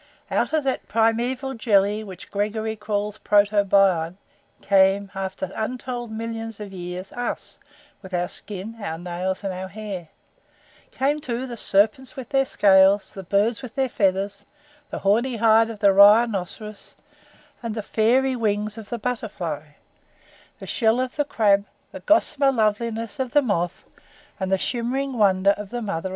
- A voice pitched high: Yes, high, 210 Hz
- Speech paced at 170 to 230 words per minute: No, average, 160 wpm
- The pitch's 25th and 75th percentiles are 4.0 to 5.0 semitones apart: No, average, 3.4 semitones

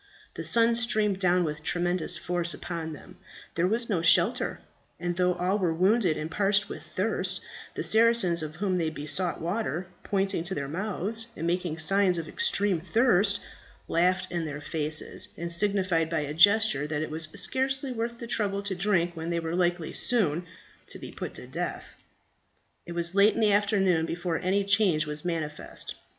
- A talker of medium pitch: Yes, medium, 180 Hz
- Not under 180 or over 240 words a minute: Yes, average, 185 wpm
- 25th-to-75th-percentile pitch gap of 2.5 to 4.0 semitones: Yes, average, 3.7 semitones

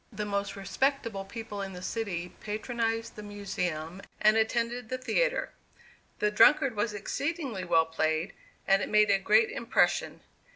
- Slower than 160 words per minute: Yes, average, 150 wpm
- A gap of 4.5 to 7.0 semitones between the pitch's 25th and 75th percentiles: No, average, 3.0 semitones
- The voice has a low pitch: No, high, 210 Hz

